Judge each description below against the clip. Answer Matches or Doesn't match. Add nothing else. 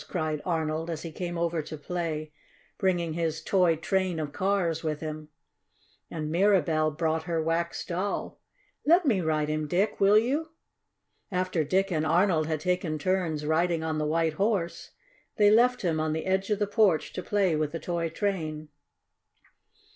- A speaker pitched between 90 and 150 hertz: Doesn't match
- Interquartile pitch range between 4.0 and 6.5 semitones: Doesn't match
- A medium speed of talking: Matches